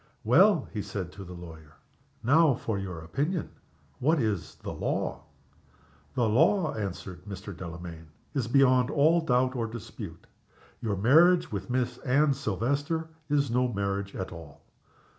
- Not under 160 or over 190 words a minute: No, average, 140 wpm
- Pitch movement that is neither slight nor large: No, wide, 6.6 semitones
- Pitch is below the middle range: Yes, low, 115 Hz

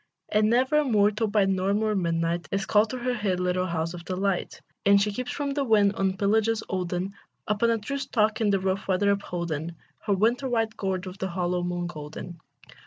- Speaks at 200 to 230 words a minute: Yes, fast, 205 wpm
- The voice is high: Yes, high, 200 Hz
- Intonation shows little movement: No, average, 3.3 semitones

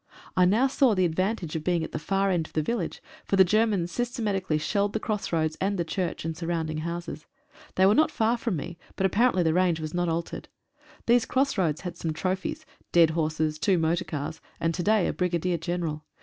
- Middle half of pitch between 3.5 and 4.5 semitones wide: Yes, average, 3.8 semitones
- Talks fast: Yes, fast, 220 wpm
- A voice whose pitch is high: No, medium, 175 Hz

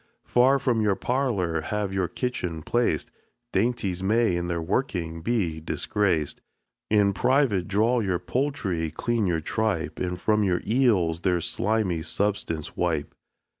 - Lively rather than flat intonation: No, average, 5.0 semitones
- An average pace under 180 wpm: Yes, slow, 135 wpm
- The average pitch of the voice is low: Yes, very low, 95 Hz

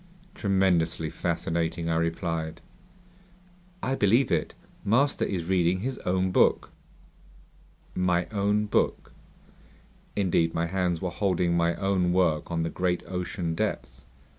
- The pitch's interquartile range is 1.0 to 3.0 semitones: Yes, narrow, 2.6 semitones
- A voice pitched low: Yes, very low, 90 Hz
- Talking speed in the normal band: No, slow, 120 wpm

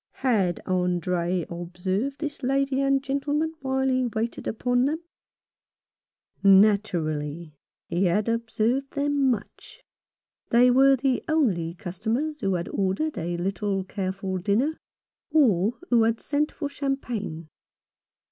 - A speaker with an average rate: No, slow, 120 wpm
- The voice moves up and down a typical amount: No, wide, 6.6 semitones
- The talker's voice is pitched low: No, high, 225 Hz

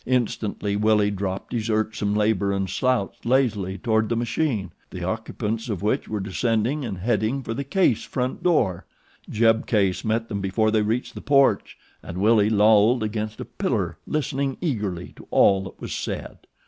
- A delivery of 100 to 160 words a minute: No, average, 170 wpm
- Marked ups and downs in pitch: No, average, 2.8 semitones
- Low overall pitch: Yes, low, 110 Hz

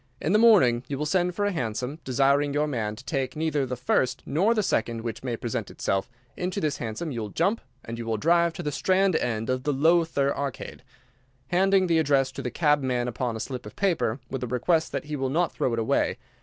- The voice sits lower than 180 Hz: Yes, medium, 140 Hz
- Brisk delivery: Yes, fast, 230 wpm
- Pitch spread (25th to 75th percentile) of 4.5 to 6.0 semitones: Yes, average, 5.3 semitones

